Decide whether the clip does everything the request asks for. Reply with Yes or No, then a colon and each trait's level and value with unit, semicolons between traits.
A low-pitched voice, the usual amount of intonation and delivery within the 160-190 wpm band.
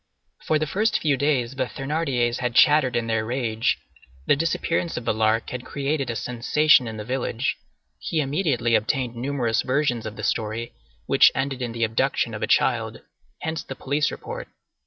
Yes: low, 130 Hz; average, 4.0 semitones; average, 180 wpm